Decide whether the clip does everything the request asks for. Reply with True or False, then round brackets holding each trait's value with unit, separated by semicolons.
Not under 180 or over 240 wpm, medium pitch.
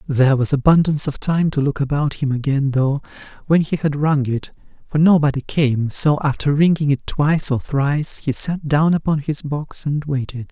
True (195 wpm; 145 Hz)